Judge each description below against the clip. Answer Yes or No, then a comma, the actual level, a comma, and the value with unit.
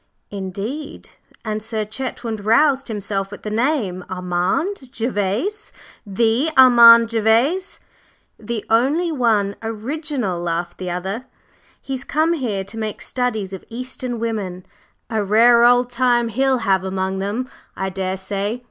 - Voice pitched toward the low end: No, high, 225 Hz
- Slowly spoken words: Yes, slow, 130 wpm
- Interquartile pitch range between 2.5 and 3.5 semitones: No, average, 4.5 semitones